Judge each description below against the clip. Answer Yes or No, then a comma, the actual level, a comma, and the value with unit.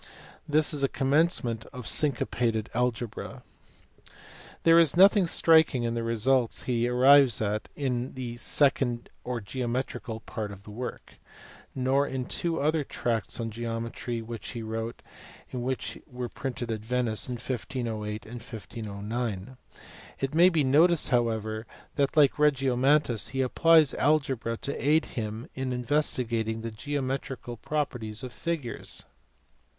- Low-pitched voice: Yes, low, 125 Hz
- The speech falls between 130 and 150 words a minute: Yes, slow, 135 wpm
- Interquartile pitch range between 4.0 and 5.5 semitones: No, average, 3.4 semitones